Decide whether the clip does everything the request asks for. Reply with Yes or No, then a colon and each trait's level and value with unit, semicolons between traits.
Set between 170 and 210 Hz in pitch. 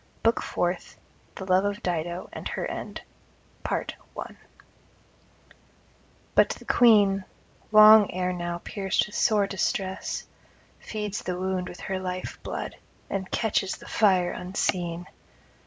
Yes: high, 190 Hz